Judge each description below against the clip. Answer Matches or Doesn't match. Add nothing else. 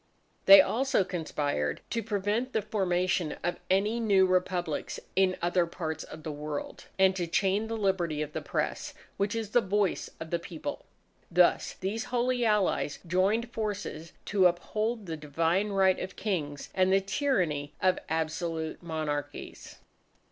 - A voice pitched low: Doesn't match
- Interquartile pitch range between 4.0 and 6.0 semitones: Matches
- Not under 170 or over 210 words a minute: Doesn't match